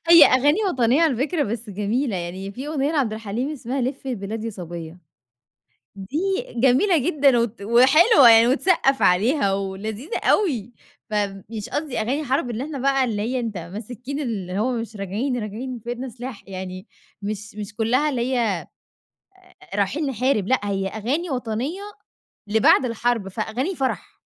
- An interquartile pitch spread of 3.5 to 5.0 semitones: Yes, average, 4.6 semitones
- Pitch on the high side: Yes, high, 235 Hz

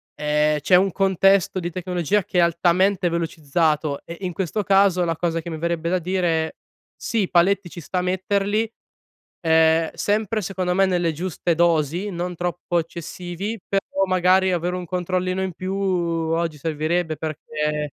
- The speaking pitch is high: No, medium, 175 Hz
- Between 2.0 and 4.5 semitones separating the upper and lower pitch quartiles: Yes, narrow, 2.4 semitones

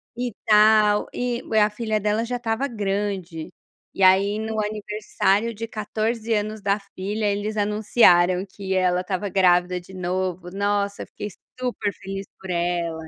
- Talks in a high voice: Yes, high, 205 Hz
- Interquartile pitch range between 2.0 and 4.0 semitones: Yes, narrow, 2.5 semitones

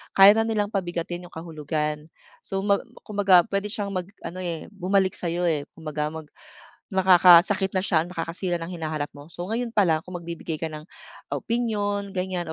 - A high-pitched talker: No, medium, 180 Hz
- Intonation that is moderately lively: Yes, average, 3.3 semitones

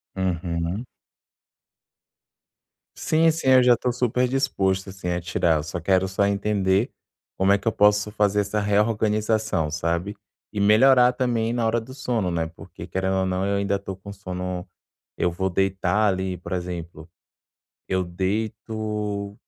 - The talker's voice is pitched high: No, low, 100 Hz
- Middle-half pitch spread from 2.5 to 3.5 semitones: Yes, average, 2.9 semitones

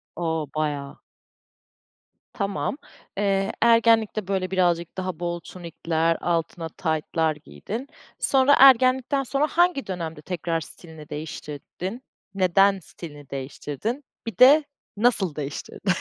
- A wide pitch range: Yes, wide, 6.2 semitones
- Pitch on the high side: No, medium, 180 Hz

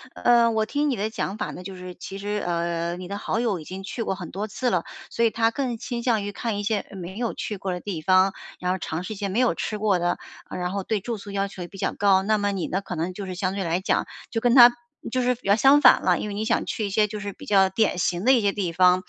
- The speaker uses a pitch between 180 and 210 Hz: Yes, high, 200 Hz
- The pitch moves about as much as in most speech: Yes, average, 3.3 semitones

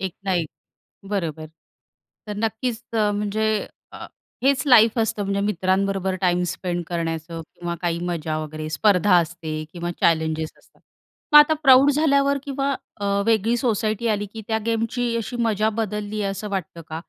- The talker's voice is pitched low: No, high, 205 Hz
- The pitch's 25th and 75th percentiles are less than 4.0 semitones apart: No, average, 4.6 semitones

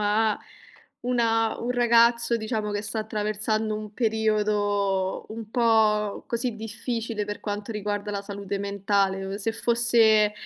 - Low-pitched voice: No, high, 215 Hz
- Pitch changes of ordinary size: No, narrow, 1.7 semitones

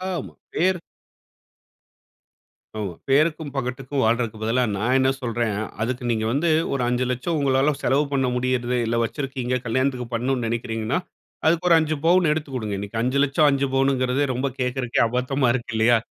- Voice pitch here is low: Yes, low, 130 Hz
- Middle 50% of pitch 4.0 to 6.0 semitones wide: No, average, 2.7 semitones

